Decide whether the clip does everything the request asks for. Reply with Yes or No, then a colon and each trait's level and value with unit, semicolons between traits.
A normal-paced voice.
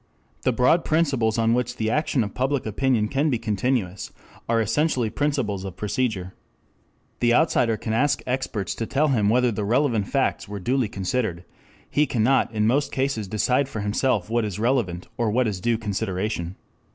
Yes: average, 175 wpm